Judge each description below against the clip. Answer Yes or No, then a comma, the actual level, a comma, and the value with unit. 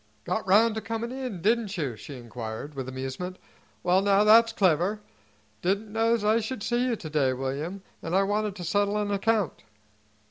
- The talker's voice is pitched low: No, high, 200 Hz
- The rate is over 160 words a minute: Yes, average, 180 wpm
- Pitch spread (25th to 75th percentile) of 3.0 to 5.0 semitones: No, wide, 5.6 semitones